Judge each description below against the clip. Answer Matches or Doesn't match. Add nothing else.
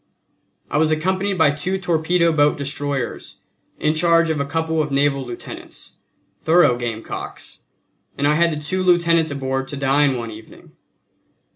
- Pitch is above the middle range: Doesn't match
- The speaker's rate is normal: Matches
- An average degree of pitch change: Matches